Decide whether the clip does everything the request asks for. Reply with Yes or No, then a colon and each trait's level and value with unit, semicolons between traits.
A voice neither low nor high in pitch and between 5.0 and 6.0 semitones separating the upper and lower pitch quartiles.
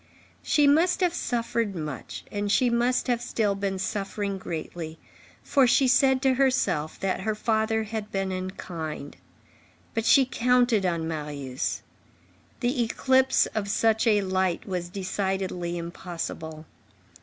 No: high, 205 Hz; wide, 5.5 semitones